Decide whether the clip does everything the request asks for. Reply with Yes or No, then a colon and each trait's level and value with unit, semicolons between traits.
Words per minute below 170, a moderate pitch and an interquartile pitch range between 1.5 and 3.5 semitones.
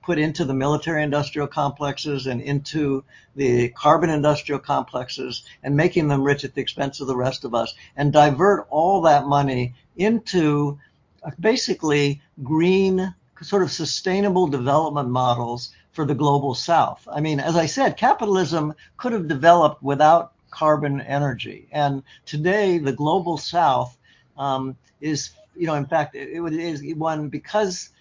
Yes: average, 150 wpm; medium, 150 Hz; average, 3.1 semitones